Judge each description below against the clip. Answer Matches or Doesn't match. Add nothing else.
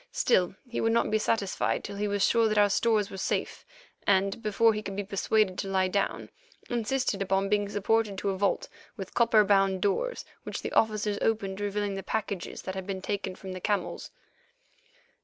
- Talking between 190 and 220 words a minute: Matches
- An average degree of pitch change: Doesn't match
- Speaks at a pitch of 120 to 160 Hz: Doesn't match